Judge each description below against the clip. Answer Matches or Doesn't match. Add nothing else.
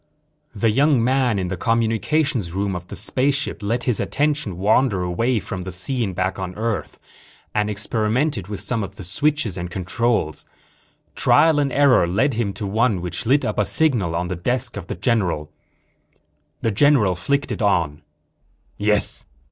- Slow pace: Doesn't match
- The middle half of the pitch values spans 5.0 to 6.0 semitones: Matches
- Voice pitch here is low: Matches